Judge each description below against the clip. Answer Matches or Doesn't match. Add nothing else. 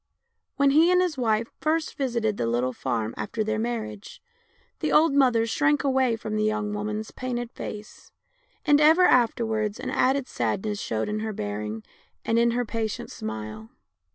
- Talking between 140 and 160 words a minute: Doesn't match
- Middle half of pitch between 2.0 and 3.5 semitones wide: Doesn't match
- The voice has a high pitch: Matches